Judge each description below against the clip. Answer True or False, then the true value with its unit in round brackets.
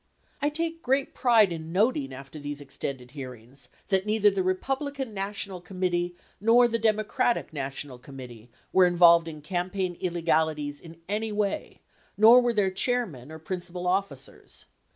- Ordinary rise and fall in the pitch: False (6.3 semitones)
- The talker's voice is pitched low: False (180 Hz)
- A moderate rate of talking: True (145 wpm)